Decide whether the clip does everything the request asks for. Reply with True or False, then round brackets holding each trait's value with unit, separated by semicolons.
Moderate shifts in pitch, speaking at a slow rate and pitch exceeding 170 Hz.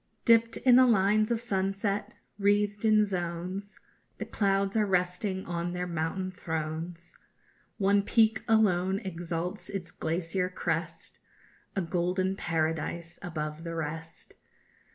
True (3.2 semitones; 120 wpm; 185 Hz)